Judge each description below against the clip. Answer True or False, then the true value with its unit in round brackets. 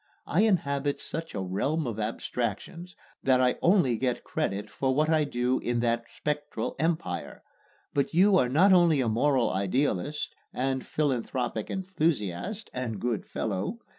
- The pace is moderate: True (145 wpm)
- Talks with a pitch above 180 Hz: False (135 Hz)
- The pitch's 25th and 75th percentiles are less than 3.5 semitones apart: False (5.3 semitones)